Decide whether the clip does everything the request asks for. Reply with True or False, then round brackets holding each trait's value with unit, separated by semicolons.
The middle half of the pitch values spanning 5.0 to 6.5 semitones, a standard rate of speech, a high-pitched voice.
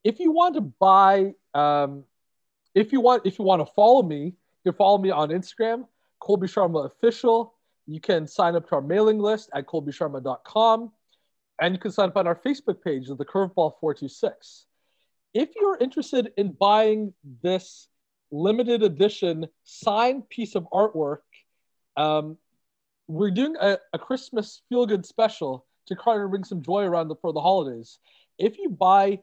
True (5.3 semitones; 170 wpm; 195 Hz)